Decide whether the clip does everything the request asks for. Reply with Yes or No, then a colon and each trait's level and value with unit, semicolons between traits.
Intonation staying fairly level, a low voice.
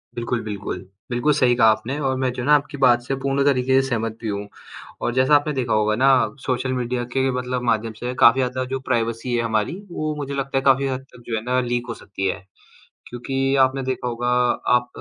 Yes: narrow, 2.3 semitones; low, 125 Hz